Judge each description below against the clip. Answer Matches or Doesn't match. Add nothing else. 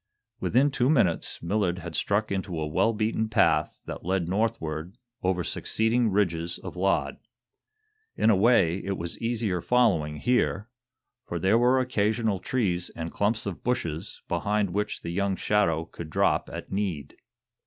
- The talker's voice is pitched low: Matches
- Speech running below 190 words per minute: Matches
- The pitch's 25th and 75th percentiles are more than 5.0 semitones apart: Doesn't match